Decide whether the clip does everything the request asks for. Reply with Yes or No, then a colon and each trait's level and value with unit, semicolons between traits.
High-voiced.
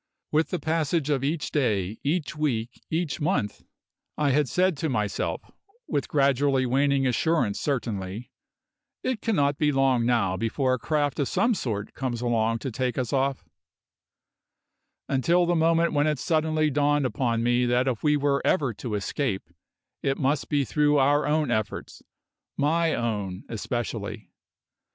No: medium, 140 Hz